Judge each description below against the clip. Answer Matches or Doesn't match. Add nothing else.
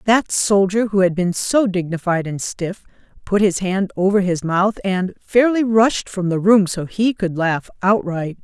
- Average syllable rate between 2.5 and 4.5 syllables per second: Matches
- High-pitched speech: Matches